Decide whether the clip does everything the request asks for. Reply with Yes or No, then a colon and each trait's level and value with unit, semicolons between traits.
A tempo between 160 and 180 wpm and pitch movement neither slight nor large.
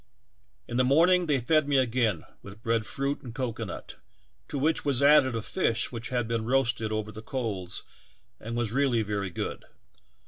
Yes: average, 175 wpm; average, 3.7 semitones